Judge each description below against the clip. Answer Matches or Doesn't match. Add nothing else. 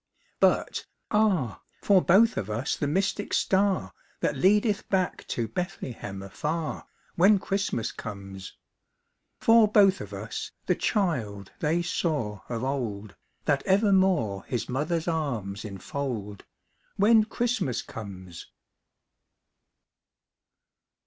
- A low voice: Doesn't match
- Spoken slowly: Matches